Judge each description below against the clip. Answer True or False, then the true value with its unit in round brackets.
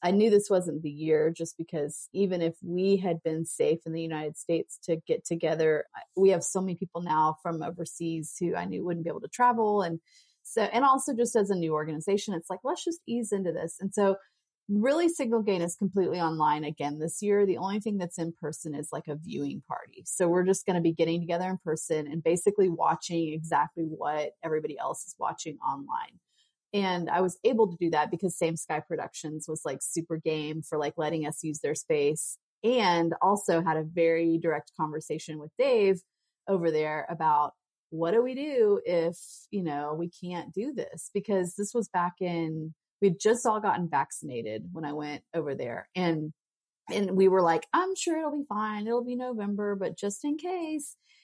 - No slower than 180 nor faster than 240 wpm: True (200 wpm)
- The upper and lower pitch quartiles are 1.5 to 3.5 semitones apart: False (4.2 semitones)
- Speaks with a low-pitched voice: False (175 Hz)